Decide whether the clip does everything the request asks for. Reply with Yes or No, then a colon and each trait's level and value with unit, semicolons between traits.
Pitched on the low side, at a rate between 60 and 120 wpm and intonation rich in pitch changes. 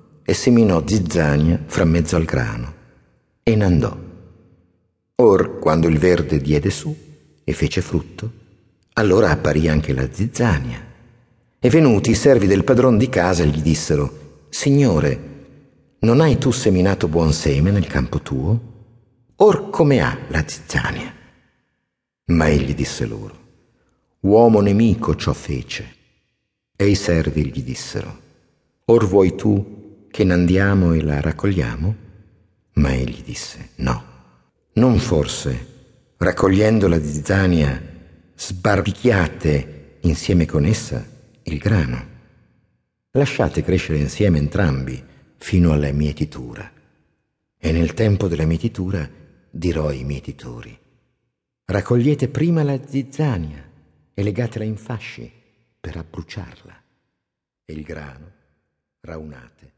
Yes: very low, 90 Hz; slow, 115 wpm; wide, 6.1 semitones